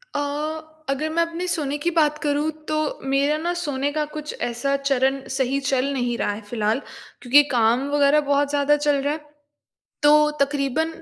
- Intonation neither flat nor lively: No, narrow, 2.0 semitones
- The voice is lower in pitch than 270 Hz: No, very high, 285 Hz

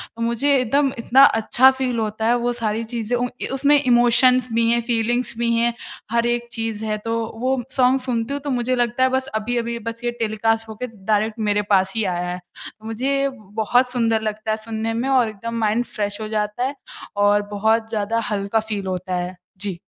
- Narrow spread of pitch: Yes, narrow, 2.2 semitones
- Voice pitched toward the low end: No, high, 230 Hz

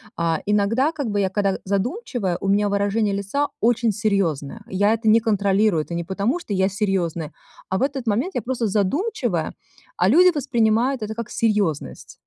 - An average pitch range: Yes, average, 3.6 semitones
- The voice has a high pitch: Yes, high, 210 Hz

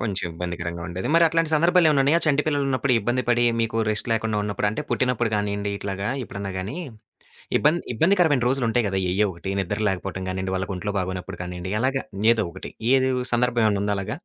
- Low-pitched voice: Yes, low, 110 Hz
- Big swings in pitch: Yes, wide, 5.8 semitones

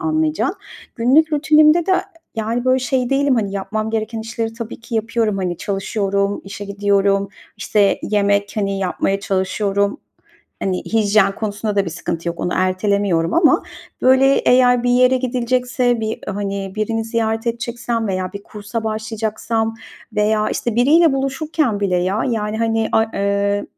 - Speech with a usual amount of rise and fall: Yes, average, 3.4 semitones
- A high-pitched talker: Yes, high, 220 Hz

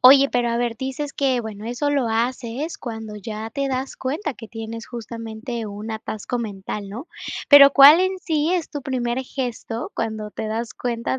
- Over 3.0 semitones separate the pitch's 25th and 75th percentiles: Yes, average, 3.6 semitones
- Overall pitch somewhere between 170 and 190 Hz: No, high, 240 Hz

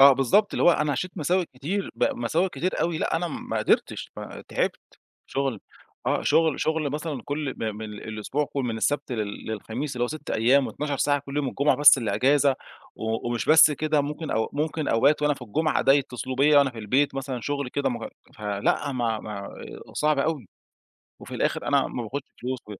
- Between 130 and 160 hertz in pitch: Yes, medium, 140 Hz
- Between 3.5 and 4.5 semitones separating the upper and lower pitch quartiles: Yes, average, 3.8 semitones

